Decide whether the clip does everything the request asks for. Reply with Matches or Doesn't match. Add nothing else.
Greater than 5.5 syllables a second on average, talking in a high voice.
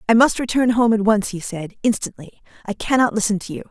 Matches